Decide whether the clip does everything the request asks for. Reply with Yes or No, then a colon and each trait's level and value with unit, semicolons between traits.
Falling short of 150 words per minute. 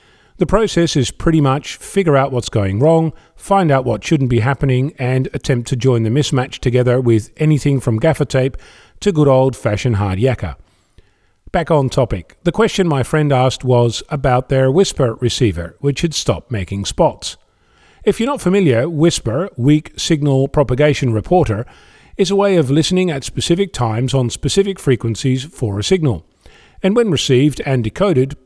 No: average, 165 wpm